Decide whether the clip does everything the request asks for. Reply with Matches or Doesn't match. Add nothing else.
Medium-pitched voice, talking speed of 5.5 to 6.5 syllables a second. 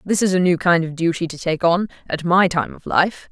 Doesn't match